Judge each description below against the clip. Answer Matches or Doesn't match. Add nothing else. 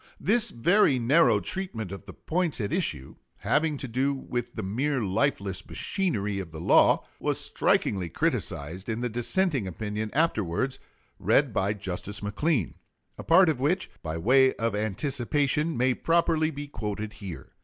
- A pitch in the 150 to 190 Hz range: Doesn't match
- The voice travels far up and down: Matches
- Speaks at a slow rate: Doesn't match